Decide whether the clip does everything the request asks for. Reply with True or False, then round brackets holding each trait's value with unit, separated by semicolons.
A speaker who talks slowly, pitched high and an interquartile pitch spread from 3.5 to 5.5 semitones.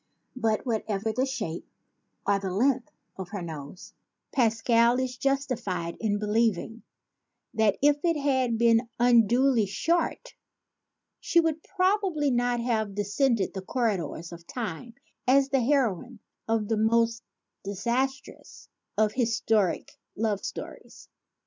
True (125 wpm; 230 Hz; 4.0 semitones)